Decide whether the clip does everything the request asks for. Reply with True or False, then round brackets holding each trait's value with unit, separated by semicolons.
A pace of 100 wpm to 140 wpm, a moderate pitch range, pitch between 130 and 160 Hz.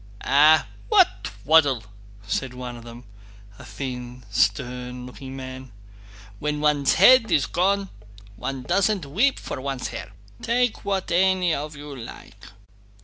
False (135 wpm; 6.4 semitones; 140 Hz)